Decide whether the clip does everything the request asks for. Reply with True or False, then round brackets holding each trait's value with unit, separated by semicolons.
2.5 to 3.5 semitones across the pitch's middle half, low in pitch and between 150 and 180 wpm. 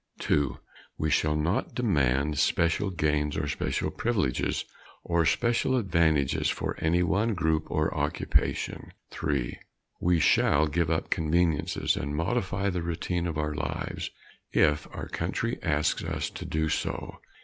False (2.9 semitones; 80 Hz; 140 wpm)